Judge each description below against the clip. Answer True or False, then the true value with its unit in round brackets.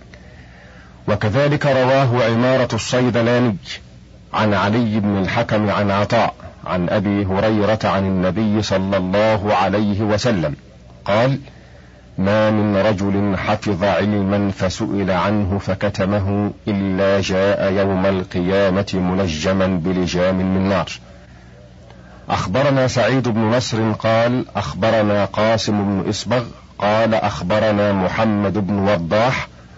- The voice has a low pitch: True (100 Hz)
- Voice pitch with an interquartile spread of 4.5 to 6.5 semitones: False (2.5 semitones)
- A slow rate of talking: False (100 wpm)